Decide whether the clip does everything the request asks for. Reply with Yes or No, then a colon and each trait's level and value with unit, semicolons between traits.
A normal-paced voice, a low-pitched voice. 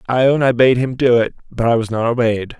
No: fast, 275 wpm; low, 120 Hz